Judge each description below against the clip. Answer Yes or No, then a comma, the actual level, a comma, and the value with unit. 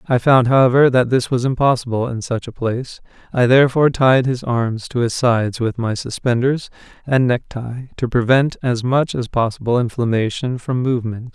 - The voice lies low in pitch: Yes, low, 125 Hz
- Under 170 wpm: No, average, 175 wpm